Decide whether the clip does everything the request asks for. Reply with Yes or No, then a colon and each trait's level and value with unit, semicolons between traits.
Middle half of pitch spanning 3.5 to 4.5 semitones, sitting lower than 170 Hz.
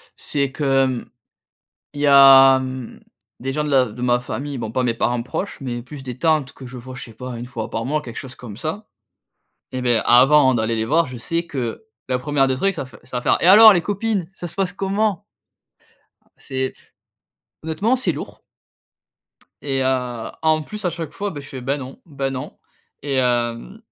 Yes: average, 4.2 semitones; low, 135 Hz